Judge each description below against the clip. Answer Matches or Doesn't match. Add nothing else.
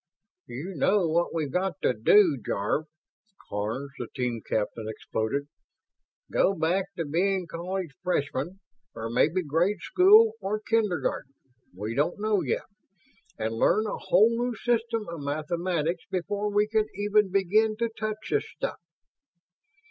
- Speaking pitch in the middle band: Matches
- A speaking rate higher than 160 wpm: Doesn't match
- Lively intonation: Matches